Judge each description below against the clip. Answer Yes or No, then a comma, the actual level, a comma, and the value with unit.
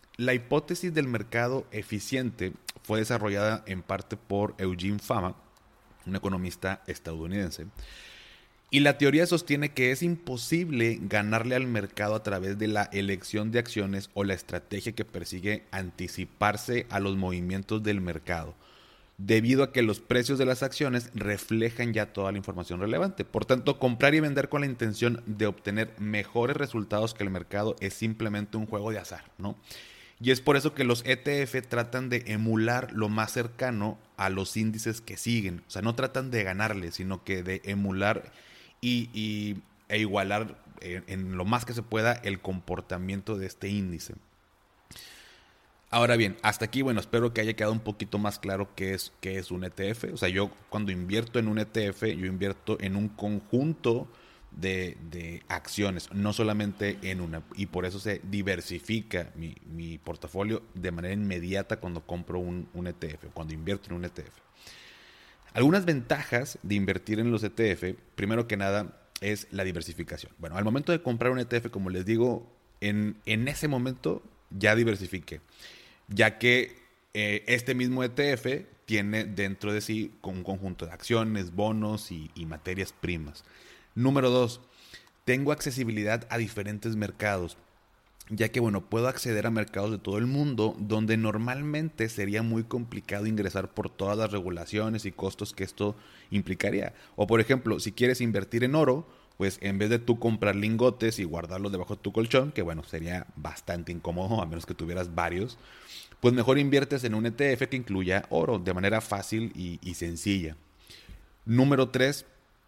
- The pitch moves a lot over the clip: No, average, 3.7 semitones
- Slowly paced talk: No, average, 165 wpm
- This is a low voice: Yes, low, 105 Hz